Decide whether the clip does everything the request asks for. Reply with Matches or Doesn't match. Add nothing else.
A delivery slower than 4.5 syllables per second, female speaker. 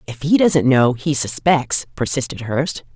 Matches